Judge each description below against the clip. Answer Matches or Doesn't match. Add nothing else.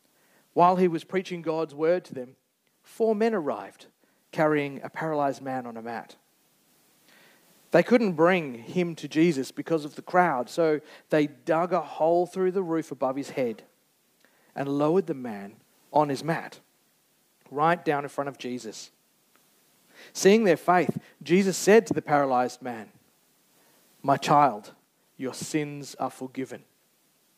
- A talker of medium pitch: Matches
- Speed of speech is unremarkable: Matches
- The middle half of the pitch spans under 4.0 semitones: Doesn't match